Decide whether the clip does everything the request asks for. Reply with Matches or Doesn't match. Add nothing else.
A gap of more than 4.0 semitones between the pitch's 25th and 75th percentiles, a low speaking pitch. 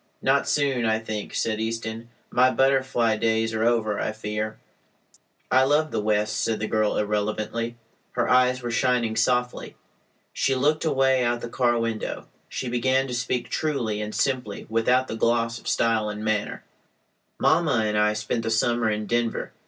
Doesn't match